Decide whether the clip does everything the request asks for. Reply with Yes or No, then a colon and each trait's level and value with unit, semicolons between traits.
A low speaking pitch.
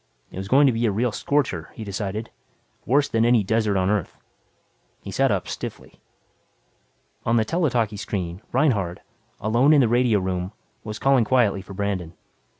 Yes: low, 110 Hz